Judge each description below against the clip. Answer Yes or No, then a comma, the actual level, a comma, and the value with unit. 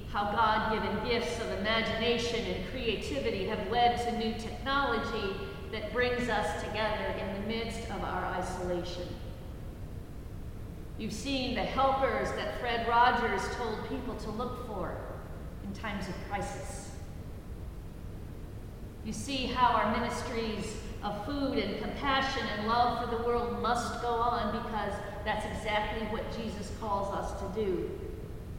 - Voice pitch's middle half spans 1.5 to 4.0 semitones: Yes, average, 2.7 semitones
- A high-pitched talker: Yes, high, 225 Hz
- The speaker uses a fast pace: No, slow, 135 wpm